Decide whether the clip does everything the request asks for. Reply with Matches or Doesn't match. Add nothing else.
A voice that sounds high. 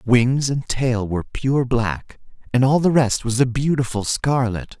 Doesn't match